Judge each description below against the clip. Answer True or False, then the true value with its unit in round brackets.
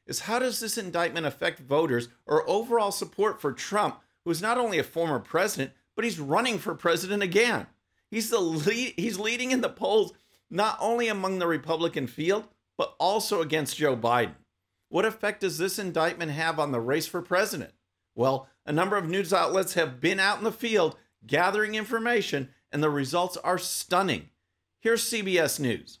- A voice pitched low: False (180 Hz)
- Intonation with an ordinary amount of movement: False (5.9 semitones)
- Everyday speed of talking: True (180 wpm)